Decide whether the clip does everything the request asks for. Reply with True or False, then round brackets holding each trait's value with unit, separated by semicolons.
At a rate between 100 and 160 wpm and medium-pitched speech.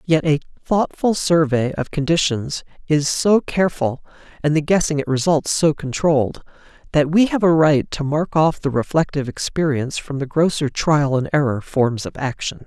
False (170 wpm; 150 Hz)